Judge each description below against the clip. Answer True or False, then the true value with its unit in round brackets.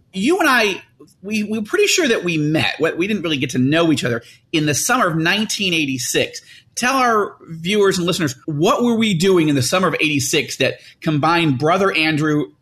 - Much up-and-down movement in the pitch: True (5.7 semitones)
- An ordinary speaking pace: True (195 wpm)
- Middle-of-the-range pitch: True (175 Hz)